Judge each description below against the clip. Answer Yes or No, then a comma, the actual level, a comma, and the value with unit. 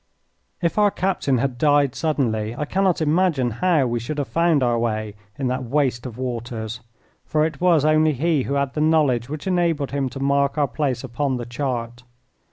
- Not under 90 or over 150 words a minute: No, average, 190 wpm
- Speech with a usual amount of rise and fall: Yes, average, 4.2 semitones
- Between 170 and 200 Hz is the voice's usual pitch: No, medium, 140 Hz